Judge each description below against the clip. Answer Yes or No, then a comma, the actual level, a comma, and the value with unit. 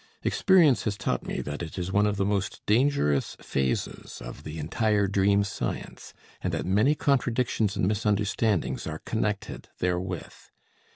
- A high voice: No, low, 100 Hz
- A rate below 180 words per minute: Yes, average, 150 wpm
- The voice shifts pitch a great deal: No, average, 3.5 semitones